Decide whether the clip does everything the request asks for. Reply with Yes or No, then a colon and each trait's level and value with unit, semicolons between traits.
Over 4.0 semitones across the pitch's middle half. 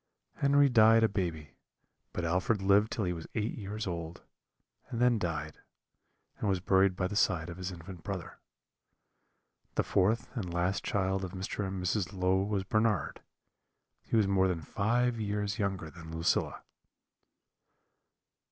No: average, 3.2 semitones